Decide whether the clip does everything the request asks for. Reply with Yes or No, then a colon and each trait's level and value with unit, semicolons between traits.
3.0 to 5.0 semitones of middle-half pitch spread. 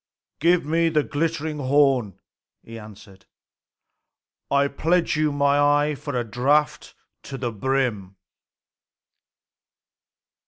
Yes: average, 3.6 semitones